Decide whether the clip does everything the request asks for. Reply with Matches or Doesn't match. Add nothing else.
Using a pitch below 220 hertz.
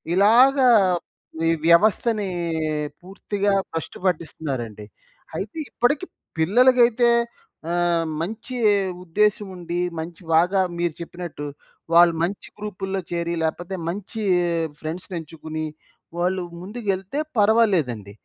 Matches